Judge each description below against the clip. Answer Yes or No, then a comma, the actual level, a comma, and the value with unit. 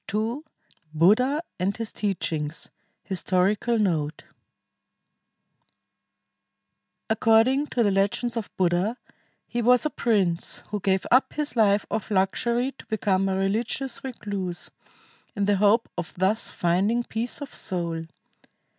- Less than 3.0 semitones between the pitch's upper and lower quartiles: No, average, 3.9 semitones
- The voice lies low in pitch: No, high, 205 Hz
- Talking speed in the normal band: No, slow, 120 wpm